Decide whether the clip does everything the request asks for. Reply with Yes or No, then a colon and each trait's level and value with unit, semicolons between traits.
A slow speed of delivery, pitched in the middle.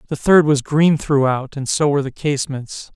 No: fast, 205 wpm; medium, 145 Hz